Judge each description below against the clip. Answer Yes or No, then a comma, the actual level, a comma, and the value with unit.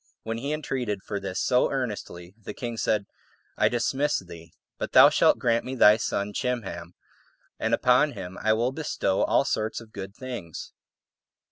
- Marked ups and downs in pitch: No, average, 4.4 semitones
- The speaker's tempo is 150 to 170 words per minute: Yes, average, 165 wpm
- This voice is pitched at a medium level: No, low, 110 Hz